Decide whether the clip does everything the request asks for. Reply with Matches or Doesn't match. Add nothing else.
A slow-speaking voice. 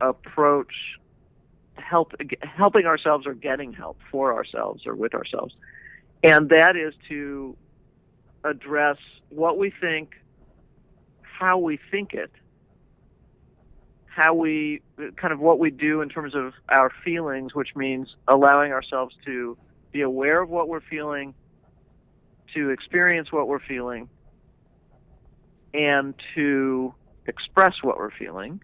Matches